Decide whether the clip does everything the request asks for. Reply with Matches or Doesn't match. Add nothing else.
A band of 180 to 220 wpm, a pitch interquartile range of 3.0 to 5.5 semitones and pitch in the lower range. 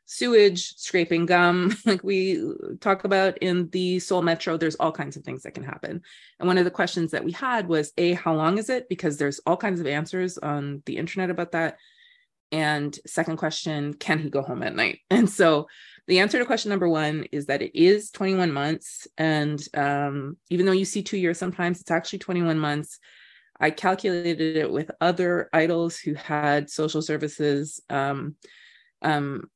Doesn't match